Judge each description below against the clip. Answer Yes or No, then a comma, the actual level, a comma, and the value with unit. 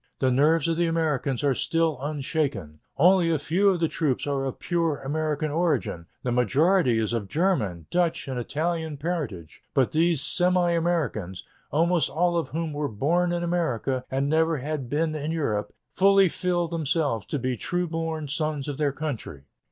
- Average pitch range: Yes, average, 3.9 semitones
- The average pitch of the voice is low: No, medium, 155 Hz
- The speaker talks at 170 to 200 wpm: Yes, average, 175 wpm